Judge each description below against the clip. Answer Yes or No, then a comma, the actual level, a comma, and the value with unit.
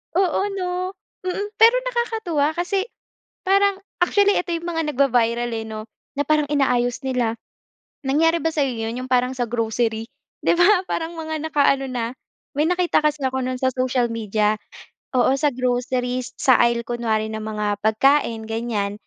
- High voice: Yes, very high, 260 Hz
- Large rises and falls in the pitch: Yes, wide, 5.7 semitones